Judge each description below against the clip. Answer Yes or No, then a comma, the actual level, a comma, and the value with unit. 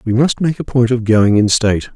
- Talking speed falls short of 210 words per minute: No, fast, 275 wpm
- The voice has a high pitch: No, low, 120 Hz